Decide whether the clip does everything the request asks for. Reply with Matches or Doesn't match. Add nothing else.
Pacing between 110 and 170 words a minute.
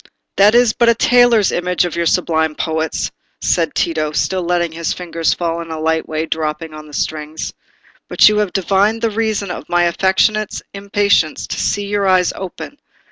Doesn't match